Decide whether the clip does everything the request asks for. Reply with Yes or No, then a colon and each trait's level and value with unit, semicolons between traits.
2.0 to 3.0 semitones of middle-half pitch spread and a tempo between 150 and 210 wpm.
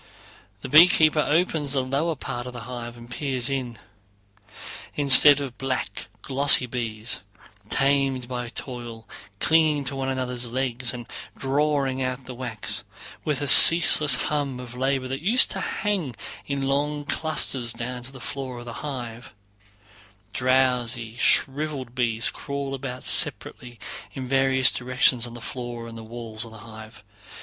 No: narrow, 2.6 semitones; average, 140 wpm